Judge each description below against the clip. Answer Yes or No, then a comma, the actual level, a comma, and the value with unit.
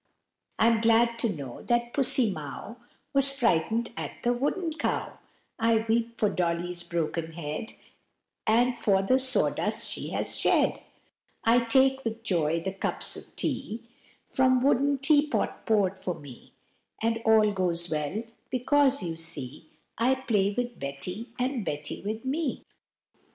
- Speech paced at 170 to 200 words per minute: No, average, 140 wpm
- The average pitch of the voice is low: No, high, 225 Hz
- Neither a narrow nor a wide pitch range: No, wide, 6.3 semitones